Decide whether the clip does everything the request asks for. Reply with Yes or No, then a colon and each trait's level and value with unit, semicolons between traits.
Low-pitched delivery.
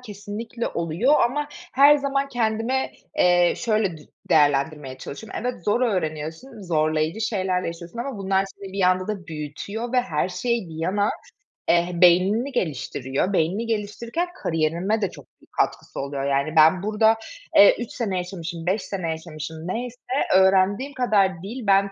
No: high, 195 Hz